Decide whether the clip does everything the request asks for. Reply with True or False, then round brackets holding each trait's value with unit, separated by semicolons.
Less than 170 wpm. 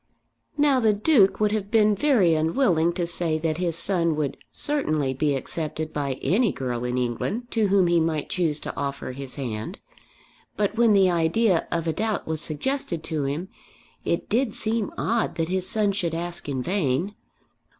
False (180 wpm)